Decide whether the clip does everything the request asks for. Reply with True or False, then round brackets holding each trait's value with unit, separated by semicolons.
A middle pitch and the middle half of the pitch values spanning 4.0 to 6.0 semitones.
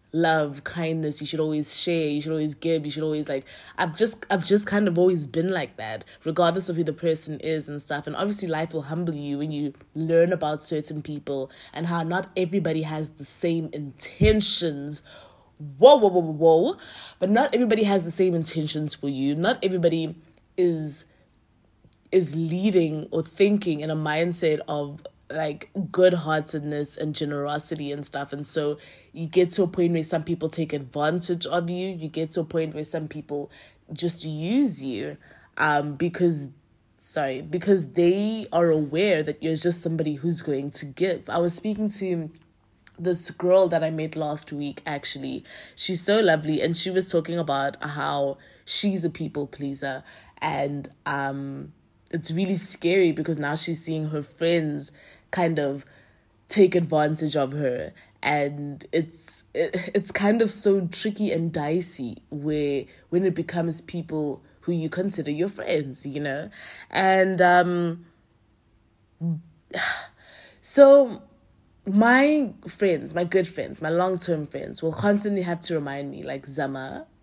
False (160 Hz; 3.2 semitones)